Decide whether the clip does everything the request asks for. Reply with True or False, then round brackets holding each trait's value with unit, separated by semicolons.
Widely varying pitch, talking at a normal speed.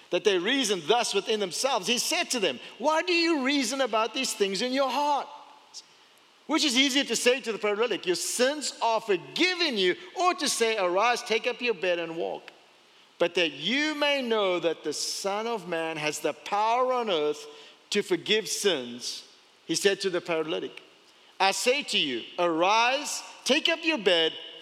True (7.1 semitones; 185 wpm)